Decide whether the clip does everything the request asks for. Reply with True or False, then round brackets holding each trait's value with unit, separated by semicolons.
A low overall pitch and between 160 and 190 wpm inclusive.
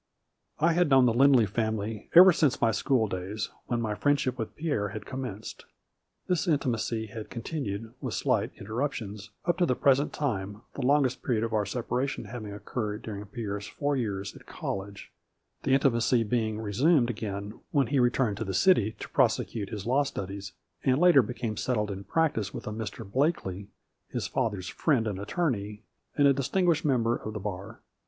True (115 Hz; 175 wpm)